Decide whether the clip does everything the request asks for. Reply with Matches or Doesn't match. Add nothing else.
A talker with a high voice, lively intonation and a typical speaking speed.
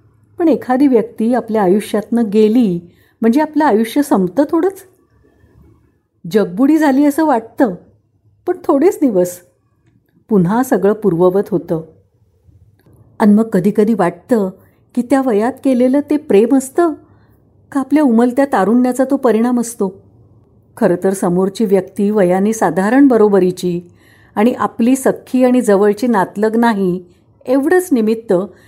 Matches